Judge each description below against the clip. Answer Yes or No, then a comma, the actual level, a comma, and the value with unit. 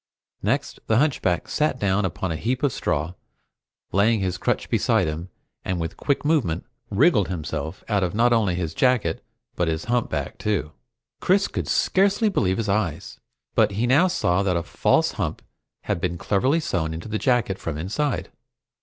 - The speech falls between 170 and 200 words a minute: Yes, average, 175 wpm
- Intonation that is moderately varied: No, wide, 6.3 semitones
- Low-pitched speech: Yes, low, 100 Hz